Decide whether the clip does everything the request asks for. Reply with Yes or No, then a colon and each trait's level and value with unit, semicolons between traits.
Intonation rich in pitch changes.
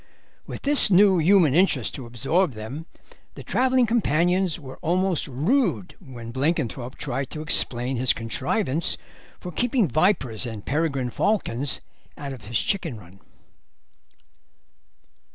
Yes: wide, 7.0 semitones